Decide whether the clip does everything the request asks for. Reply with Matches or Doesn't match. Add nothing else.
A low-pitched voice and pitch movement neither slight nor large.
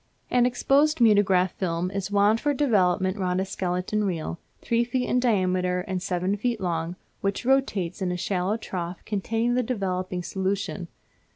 Doesn't match